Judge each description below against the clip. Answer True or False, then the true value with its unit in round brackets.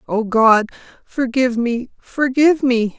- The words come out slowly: True (80 wpm)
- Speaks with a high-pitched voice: True (245 Hz)